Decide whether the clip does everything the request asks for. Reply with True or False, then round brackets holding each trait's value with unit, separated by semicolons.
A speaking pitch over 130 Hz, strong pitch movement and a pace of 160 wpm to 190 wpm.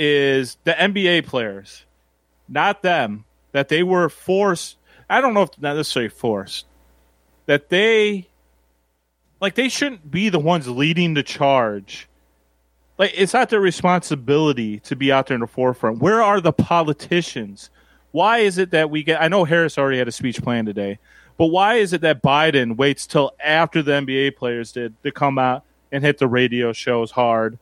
True (140 Hz; 6.9 semitones; 175 wpm)